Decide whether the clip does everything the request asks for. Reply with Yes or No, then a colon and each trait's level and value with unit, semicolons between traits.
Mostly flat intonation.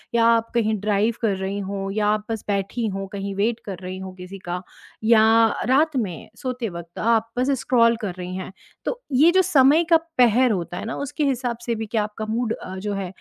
No: average, 3.6 semitones